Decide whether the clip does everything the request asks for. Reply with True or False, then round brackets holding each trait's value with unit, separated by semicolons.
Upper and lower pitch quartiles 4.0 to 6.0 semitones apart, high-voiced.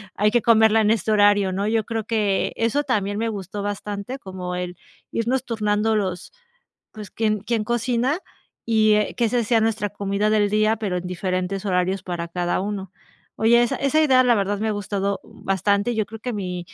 False (2.5 semitones; 210 Hz)